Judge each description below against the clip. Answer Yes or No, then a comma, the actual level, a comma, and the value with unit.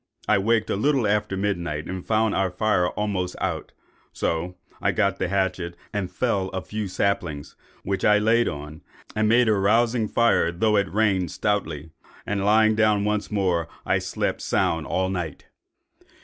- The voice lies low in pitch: Yes, low, 100 Hz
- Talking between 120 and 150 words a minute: No, average, 165 wpm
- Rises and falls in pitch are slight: No, average, 3.0 semitones